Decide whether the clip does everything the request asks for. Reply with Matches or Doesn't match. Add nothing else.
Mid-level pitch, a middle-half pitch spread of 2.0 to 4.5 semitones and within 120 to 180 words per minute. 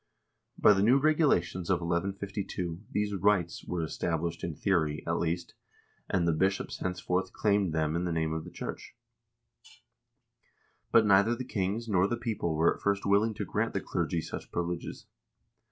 Doesn't match